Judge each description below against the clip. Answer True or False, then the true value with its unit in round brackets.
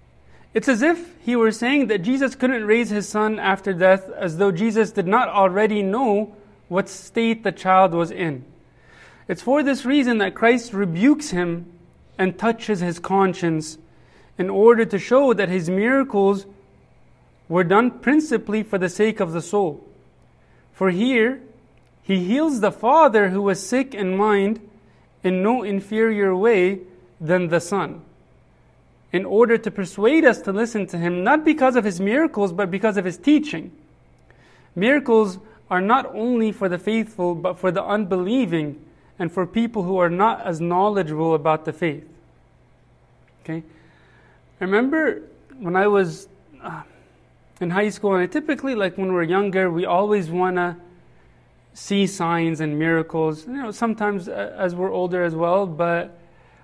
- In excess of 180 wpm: False (155 wpm)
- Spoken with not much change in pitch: False (4.1 semitones)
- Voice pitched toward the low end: False (195 Hz)